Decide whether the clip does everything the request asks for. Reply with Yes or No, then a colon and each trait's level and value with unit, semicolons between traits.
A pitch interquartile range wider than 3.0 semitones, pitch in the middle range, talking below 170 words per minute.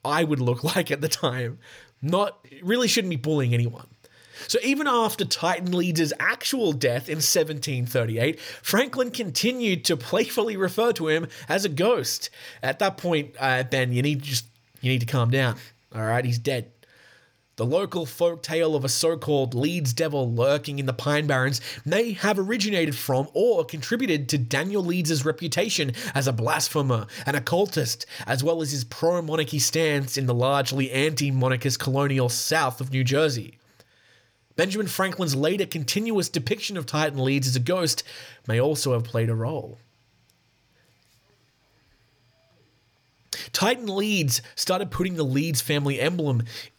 Yes: average, 5.2 semitones; medium, 145 Hz; average, 155 wpm